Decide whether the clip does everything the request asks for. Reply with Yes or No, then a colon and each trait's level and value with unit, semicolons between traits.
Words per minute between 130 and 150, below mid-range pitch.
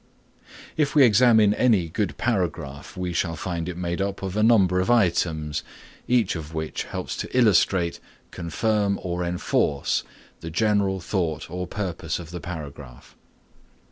Yes: average, 145 wpm; very low, 90 Hz